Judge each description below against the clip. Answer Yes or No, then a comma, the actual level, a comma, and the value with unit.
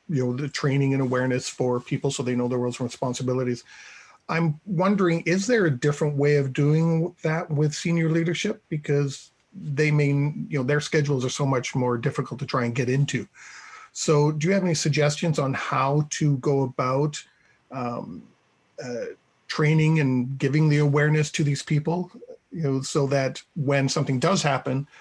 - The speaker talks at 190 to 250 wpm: No, average, 180 wpm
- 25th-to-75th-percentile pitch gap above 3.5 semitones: No, average, 2.9 semitones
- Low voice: No, medium, 145 Hz